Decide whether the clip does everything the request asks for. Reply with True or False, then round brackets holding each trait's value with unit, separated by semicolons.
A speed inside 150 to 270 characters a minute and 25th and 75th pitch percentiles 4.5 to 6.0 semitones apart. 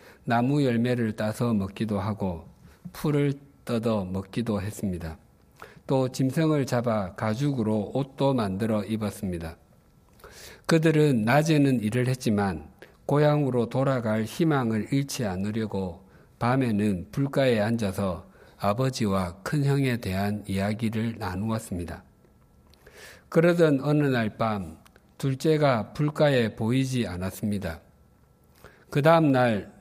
True (250 characters per minute; 5.2 semitones)